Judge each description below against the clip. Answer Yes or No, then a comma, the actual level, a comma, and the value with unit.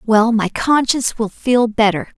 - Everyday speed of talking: Yes, average, 165 wpm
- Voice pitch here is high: Yes, high, 225 Hz